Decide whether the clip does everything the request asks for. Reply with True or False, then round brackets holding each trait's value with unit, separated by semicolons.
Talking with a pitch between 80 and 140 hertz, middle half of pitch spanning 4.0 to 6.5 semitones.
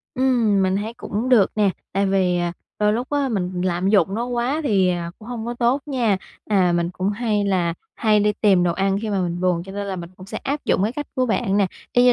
False (205 Hz; 4.3 semitones)